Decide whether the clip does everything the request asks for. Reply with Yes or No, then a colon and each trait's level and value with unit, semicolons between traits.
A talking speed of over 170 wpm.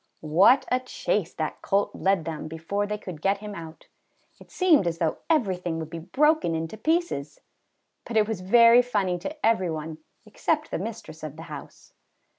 Yes: average, 180 wpm